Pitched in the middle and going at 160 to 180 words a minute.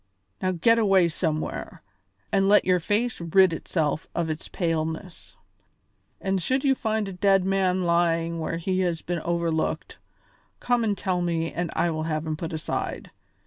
Yes: medium, 175 Hz; average, 165 wpm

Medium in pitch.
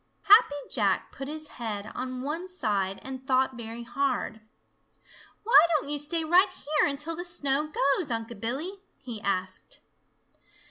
No: very high, 270 Hz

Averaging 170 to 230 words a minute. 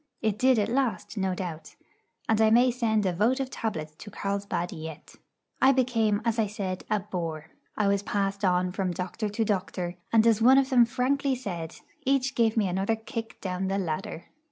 Yes: average, 190 wpm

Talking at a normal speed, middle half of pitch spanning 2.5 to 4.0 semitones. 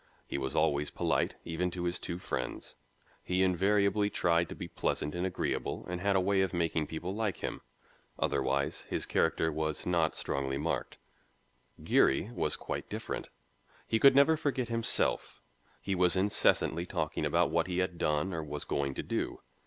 Yes: average, 170 wpm; average, 3.5 semitones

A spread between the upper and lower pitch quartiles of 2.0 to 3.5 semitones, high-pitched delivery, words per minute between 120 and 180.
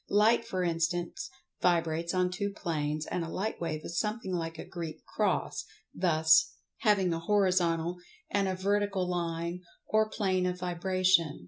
No: narrow, 2.5 semitones; medium, 180 Hz; average, 165 wpm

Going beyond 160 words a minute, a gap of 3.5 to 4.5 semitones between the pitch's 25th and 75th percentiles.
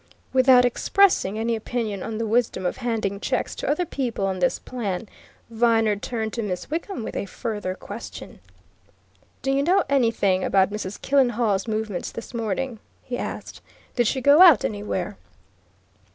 No: average, 155 wpm; average, 3.8 semitones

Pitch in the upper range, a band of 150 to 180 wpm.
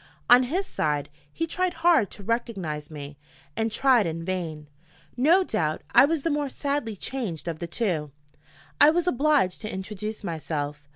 Yes: high, 215 Hz; average, 165 wpm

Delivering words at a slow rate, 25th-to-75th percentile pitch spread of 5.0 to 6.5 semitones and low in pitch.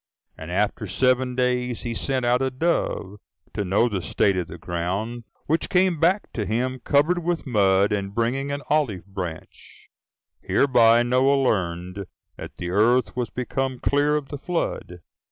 No: average, 160 wpm; wide, 5.5 semitones; low, 120 Hz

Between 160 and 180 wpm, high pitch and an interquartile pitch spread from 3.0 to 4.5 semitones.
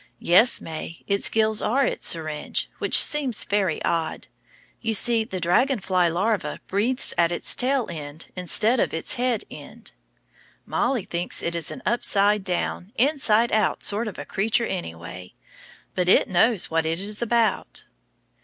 No: average, 165 wpm; high, 200 Hz; wide, 5.4 semitones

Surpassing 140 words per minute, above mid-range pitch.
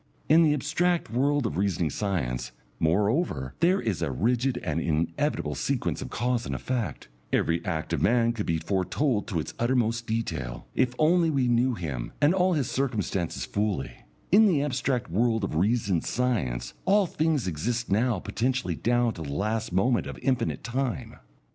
No: average, 165 wpm; low, 115 Hz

